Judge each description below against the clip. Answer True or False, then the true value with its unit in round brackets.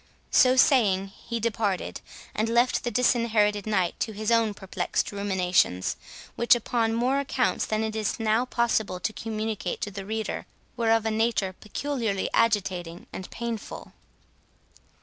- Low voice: False (220 Hz)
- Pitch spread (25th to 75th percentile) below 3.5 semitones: True (2.7 semitones)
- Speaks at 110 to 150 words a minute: True (145 wpm)